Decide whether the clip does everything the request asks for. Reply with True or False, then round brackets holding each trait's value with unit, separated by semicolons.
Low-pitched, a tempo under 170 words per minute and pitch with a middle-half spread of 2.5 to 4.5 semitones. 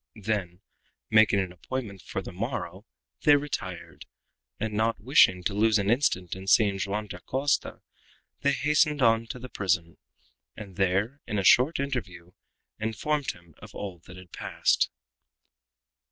False (105 Hz; 145 wpm; 5.1 semitones)